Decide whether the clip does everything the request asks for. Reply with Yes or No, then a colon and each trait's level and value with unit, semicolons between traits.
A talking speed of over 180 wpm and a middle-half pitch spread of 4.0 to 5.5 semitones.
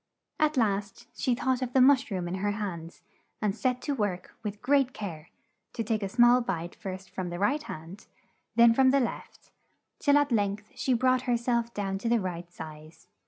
Yes: average, 200 wpm; average, 4.8 semitones